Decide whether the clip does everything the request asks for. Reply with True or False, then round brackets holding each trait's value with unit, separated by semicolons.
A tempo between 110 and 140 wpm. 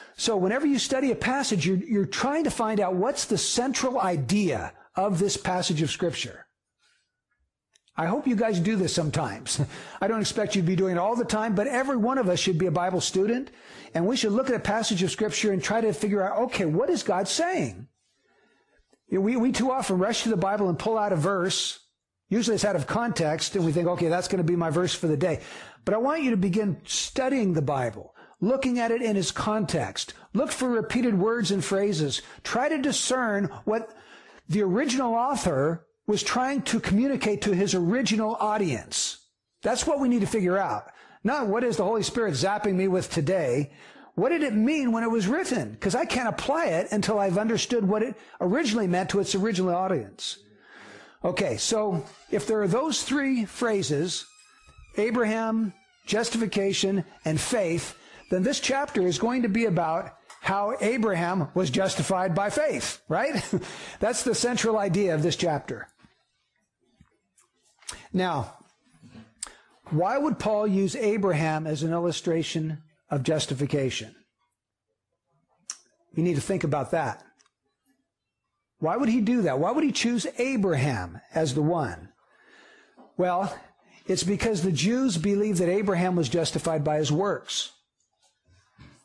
False (170 wpm)